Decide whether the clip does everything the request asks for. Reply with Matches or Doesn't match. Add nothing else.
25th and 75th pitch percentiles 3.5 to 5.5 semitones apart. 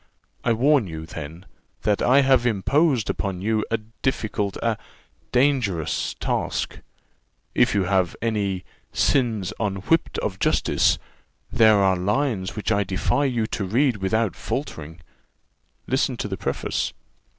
Matches